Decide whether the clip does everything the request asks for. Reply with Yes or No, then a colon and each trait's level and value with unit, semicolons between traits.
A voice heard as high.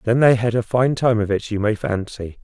No: low, 115 Hz